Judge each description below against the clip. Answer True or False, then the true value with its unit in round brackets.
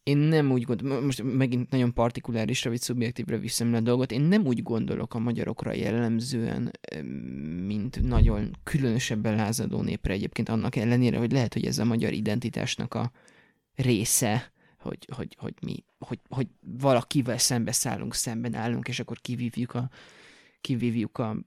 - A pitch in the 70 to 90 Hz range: False (120 Hz)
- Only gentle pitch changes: True (1.9 semitones)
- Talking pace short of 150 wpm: False (155 wpm)